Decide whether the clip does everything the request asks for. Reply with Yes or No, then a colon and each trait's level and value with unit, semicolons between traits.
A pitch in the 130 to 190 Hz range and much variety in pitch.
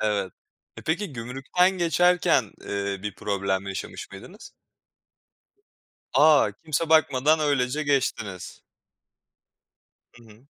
Yes: low, 135 Hz; wide, 7.6 semitones